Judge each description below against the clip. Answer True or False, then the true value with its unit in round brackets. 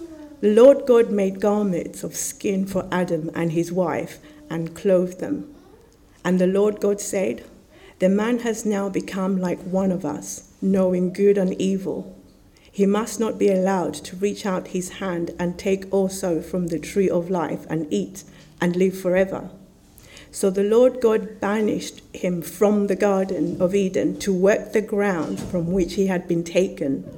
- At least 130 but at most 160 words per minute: False (170 wpm)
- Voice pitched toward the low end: False (190 Hz)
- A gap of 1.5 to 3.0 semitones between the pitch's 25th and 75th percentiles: True (2.6 semitones)